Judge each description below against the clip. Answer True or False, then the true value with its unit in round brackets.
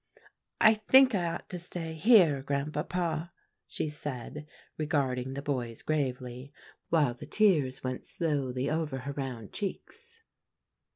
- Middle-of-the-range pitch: True (150 Hz)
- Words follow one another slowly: True (125 wpm)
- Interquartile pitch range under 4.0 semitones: False (4.6 semitones)